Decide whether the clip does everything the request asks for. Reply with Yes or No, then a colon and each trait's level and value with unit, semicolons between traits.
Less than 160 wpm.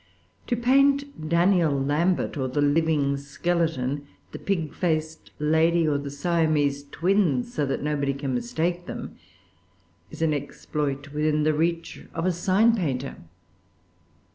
Yes: slow, 135 wpm